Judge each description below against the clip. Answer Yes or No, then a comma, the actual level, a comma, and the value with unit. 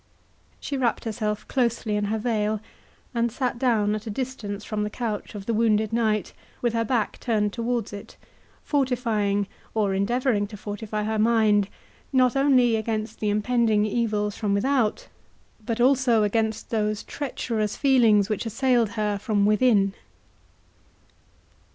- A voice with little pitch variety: Yes, narrow, 2.3 semitones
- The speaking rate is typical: Yes, average, 145 wpm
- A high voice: Yes, high, 220 Hz